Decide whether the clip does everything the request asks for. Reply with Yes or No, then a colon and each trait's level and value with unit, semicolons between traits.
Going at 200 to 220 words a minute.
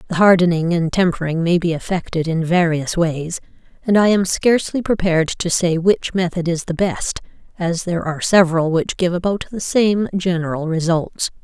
No: average, 175 wpm